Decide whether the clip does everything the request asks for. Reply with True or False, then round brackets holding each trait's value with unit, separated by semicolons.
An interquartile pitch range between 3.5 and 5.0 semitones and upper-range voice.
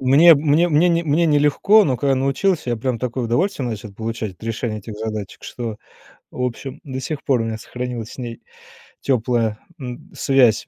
False (4.2 semitones; 125 Hz)